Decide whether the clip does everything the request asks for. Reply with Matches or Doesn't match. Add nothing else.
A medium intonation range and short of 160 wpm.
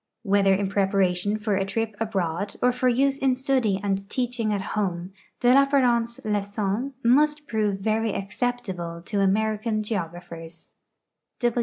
Matches